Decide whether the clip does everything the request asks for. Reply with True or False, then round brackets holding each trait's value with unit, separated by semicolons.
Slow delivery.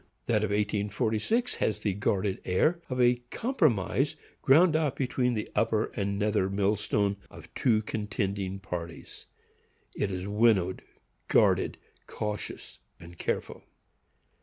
True (115 wpm)